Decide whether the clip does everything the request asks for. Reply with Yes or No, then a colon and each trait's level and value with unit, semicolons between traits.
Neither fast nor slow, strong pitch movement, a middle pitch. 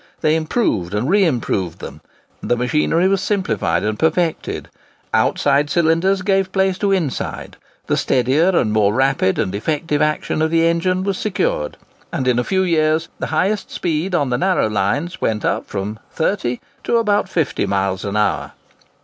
Yes: average, 170 wpm; wide, 8.5 semitones; medium, 155 Hz